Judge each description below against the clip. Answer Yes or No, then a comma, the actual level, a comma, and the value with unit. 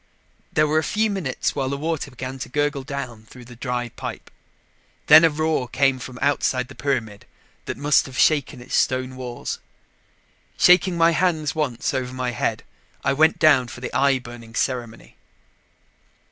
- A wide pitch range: No, average, 3.4 semitones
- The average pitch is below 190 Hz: Yes, low, 135 Hz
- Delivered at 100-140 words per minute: No, average, 170 wpm